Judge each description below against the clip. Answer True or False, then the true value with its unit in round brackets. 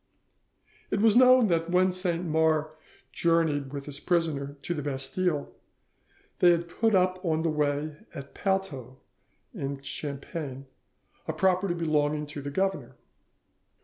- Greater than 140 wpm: False (135 wpm)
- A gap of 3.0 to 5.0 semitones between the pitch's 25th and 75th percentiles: True (4.2 semitones)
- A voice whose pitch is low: False (160 Hz)